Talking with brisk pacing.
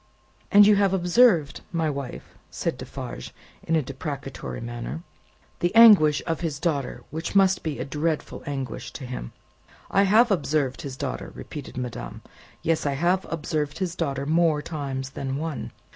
No: average, 160 wpm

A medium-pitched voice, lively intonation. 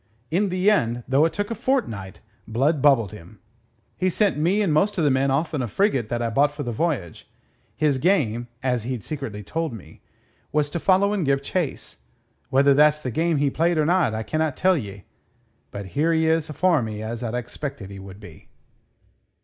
Yes: medium, 145 Hz; wide, 6.1 semitones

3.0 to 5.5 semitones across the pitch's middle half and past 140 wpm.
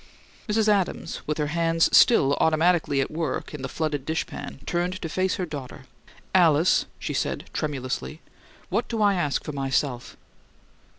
Yes: average, 3.9 semitones; average, 155 wpm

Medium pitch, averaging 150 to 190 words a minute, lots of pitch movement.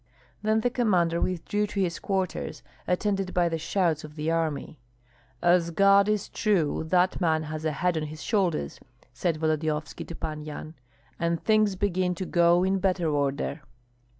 No: medium, 170 Hz; average, 165 wpm; average, 3.6 semitones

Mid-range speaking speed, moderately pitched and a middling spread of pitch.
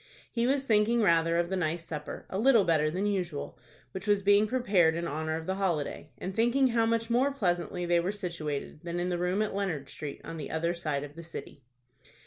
No: fast, 210 wpm; medium, 175 Hz; average, 4.5 semitones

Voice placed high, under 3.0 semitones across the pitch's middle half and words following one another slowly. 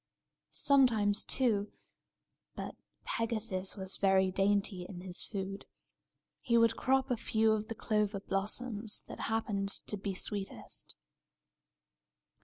Yes: high, 205 Hz; narrow, 2.6 semitones; slow, 115 wpm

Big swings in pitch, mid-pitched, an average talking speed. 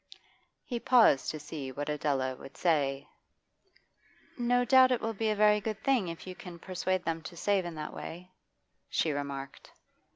Yes: wide, 6.7 semitones; medium, 175 Hz; average, 170 wpm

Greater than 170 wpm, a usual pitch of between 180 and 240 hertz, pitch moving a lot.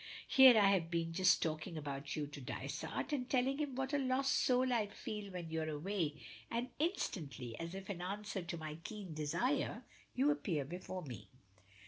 Yes: average, 180 wpm; medium, 185 Hz; wide, 8.0 semitones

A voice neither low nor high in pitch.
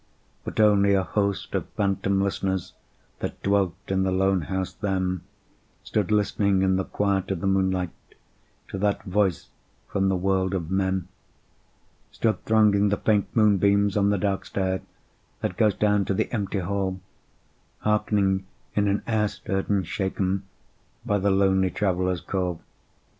No: very low, 95 Hz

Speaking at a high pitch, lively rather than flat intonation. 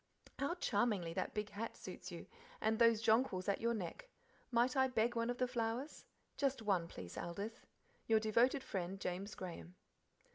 No: high, 225 Hz; average, 3.7 semitones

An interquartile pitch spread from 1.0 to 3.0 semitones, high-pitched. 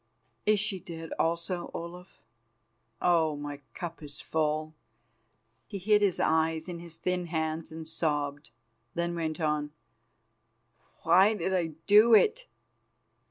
No: narrow, 2.5 semitones; medium, 165 Hz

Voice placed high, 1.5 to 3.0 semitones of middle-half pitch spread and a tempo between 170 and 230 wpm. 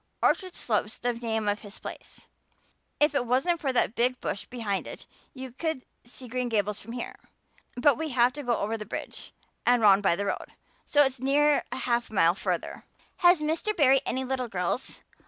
No: high, 245 Hz; average, 3.9 semitones; average, 190 wpm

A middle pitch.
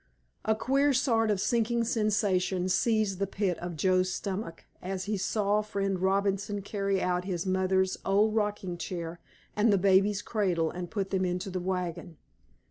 No: high, 195 Hz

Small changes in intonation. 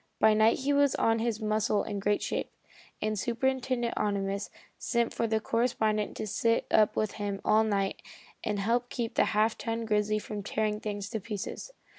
Yes: narrow, 1.8 semitones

